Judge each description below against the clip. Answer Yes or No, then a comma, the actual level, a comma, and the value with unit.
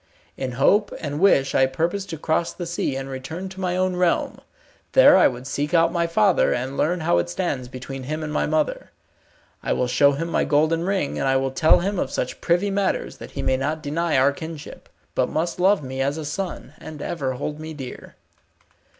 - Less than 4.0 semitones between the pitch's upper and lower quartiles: No, average, 4.5 semitones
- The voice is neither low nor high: Yes, medium, 155 Hz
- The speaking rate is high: Yes, fast, 215 wpm